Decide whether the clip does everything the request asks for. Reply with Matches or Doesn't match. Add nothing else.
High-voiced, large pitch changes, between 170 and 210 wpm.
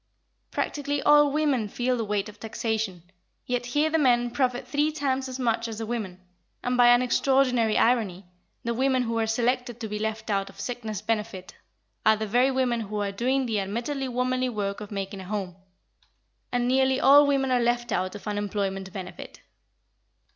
Doesn't match